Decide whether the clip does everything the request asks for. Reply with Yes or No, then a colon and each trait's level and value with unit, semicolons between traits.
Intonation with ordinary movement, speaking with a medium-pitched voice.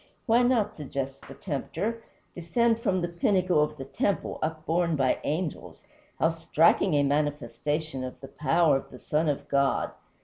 Yes: average, 4.0 semitones; medium, 155 Hz